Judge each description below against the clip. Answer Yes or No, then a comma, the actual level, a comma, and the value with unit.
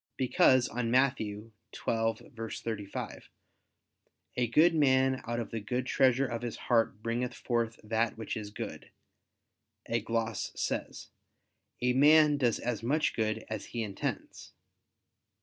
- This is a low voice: Yes, low, 115 Hz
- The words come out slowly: Yes, slow, 130 wpm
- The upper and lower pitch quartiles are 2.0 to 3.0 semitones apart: Yes, narrow, 2.4 semitones